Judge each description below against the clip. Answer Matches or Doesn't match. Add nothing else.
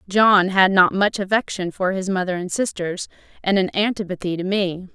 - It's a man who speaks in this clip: Doesn't match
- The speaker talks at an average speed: Matches